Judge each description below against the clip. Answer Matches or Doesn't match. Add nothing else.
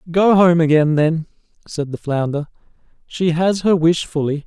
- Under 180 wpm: Matches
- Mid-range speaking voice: Matches